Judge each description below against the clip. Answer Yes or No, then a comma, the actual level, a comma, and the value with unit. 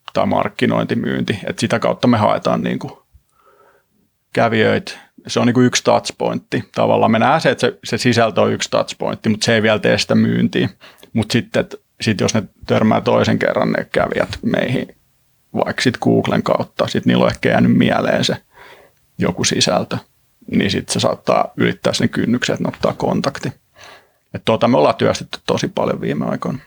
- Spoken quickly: Yes, fast, 165 wpm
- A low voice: Yes, low, 110 Hz